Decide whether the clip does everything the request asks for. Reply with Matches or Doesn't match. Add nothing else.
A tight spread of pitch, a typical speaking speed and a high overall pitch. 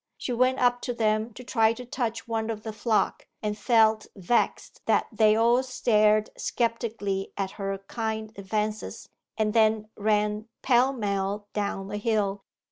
Matches